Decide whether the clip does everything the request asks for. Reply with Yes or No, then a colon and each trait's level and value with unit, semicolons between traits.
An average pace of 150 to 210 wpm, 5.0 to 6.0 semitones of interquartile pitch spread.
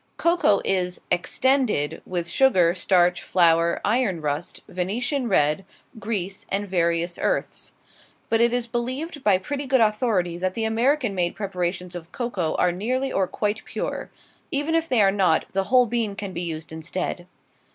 Yes: average, 160 wpm; wide, 5.5 semitones